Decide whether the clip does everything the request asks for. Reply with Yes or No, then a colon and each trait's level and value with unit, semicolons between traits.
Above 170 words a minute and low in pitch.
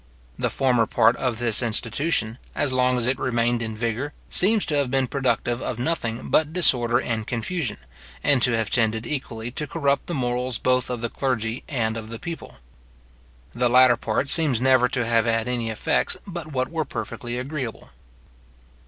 Yes: average, 180 wpm; low, 125 Hz